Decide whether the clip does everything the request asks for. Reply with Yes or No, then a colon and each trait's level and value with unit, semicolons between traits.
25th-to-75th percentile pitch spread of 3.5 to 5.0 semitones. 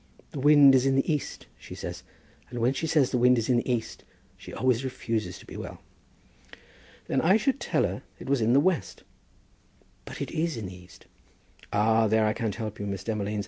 Yes: average, 4.1 semitones